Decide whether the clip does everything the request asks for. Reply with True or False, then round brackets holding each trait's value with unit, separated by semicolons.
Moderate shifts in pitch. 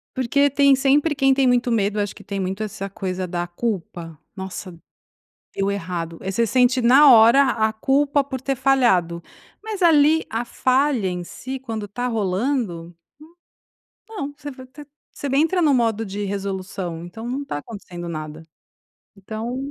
False (6.1 semitones)